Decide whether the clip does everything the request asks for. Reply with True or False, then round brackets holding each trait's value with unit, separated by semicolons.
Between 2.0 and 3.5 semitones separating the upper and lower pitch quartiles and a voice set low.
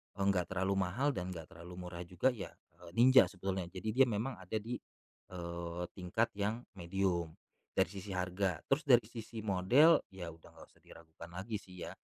False (4.0 semitones; 95 Hz)